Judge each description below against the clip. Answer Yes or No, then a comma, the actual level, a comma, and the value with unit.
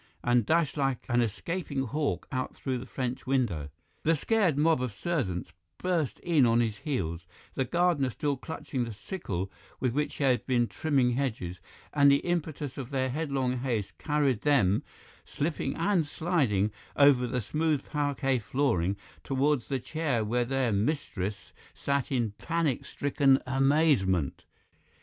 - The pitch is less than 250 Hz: Yes, low, 135 Hz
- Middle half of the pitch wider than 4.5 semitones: No, average, 3.9 semitones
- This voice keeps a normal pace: Yes, average, 150 wpm